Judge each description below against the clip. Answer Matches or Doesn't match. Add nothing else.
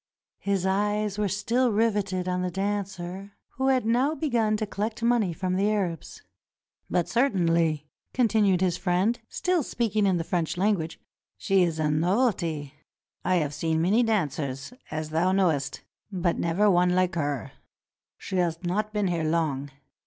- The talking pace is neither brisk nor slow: Matches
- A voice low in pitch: Doesn't match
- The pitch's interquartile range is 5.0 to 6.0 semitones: Doesn't match